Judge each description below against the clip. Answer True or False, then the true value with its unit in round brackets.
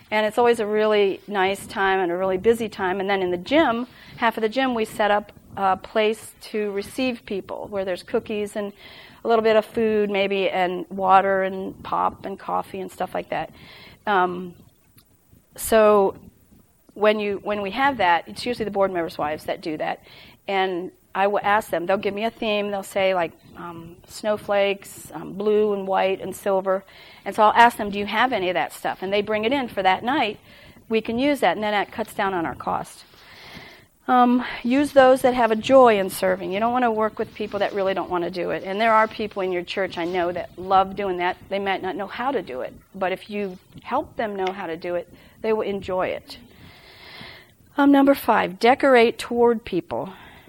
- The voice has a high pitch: True (205 Hz)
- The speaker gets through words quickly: True (215 wpm)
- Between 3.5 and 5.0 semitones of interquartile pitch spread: False (3.0 semitones)